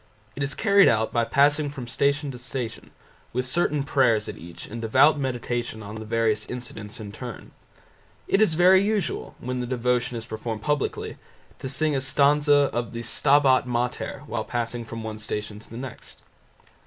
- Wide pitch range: No, average, 3.9 semitones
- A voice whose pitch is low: Yes, low, 125 Hz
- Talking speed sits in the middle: Yes, average, 180 wpm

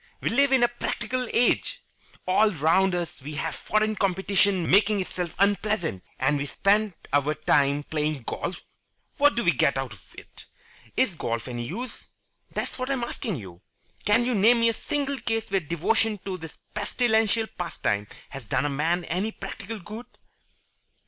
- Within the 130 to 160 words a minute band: No, average, 170 wpm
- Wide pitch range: Yes, wide, 6.6 semitones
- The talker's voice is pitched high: Yes, high, 195 Hz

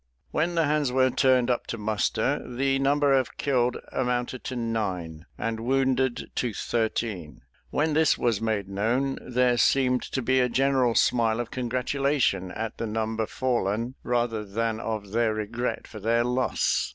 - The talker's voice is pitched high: No, low, 120 Hz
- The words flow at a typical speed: Yes, average, 160 wpm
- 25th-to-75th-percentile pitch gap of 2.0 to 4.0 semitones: Yes, average, 2.9 semitones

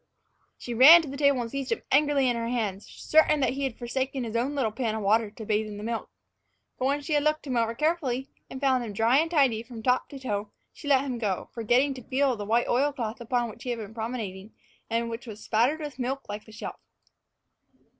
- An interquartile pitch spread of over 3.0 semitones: Yes, average, 3.6 semitones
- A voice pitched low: No, high, 245 Hz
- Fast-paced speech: Yes, fast, 245 wpm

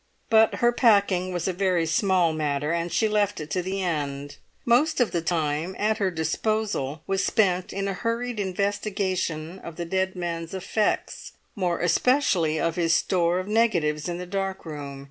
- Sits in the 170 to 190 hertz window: Yes, medium, 185 Hz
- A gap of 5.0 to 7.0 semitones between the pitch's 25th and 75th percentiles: No, average, 3.7 semitones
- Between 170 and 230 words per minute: Yes, average, 175 wpm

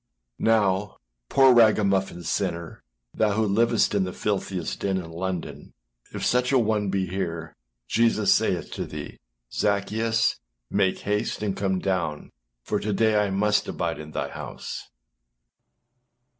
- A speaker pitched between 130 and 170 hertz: No, low, 100 Hz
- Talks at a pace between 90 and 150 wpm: Yes, average, 140 wpm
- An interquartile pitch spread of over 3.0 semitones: No, average, 2.7 semitones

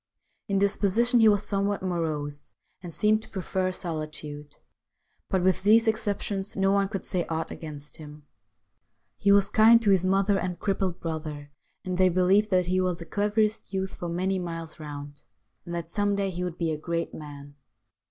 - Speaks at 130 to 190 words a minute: Yes, average, 180 wpm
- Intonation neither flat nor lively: Yes, average, 3.6 semitones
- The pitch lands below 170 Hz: No, medium, 185 Hz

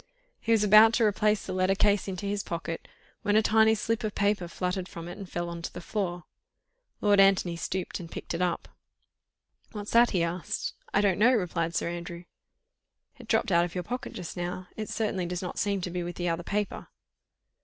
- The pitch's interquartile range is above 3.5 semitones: No, average, 3.1 semitones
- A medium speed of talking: No, fast, 210 wpm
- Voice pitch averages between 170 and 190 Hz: Yes, medium, 185 Hz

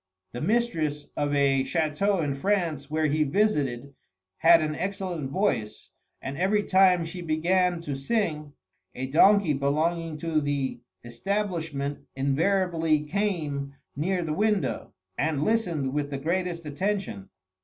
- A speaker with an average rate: No, slow, 130 wpm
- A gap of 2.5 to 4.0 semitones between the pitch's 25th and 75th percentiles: No, average, 4.7 semitones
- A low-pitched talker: No, medium, 160 Hz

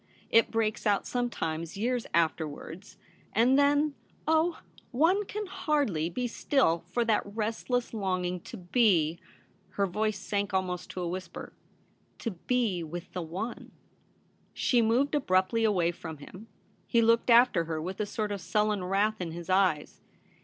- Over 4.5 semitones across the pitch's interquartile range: Yes, average, 5.1 semitones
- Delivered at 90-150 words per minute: No, average, 165 wpm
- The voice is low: No, high, 205 Hz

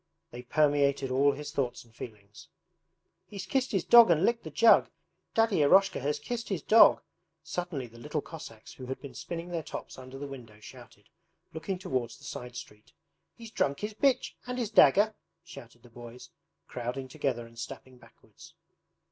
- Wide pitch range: Yes, wide, 7.5 semitones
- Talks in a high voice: No, medium, 145 Hz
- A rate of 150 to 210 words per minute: Yes, average, 175 wpm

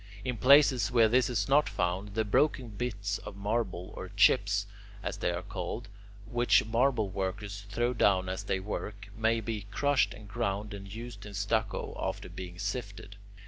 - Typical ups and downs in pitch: Yes, average, 3.2 semitones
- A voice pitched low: Yes, low, 105 Hz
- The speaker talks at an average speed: Yes, average, 170 wpm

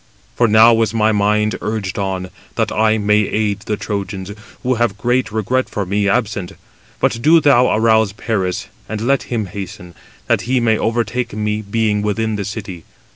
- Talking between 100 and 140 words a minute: No, average, 180 wpm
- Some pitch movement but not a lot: No, narrow, 2.2 semitones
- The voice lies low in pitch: Yes, low, 110 Hz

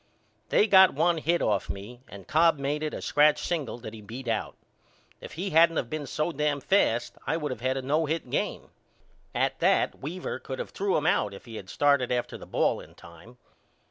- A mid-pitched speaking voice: Yes, medium, 145 Hz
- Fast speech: Yes, fast, 215 wpm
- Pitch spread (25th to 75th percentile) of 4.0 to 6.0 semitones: Yes, average, 5.2 semitones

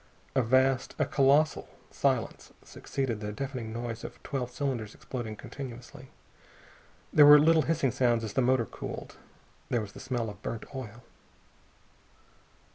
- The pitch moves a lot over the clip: No, average, 3.0 semitones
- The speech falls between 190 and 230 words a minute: No, average, 140 wpm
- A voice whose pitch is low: Yes, low, 125 Hz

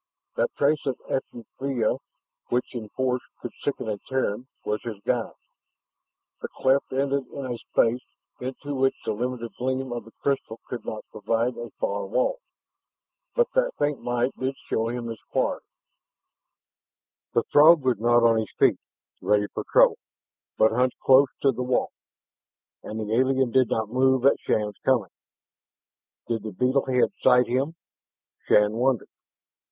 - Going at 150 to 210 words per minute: Yes, average, 155 wpm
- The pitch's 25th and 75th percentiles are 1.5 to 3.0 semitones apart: Yes, average, 2.7 semitones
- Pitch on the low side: Yes, low, 125 Hz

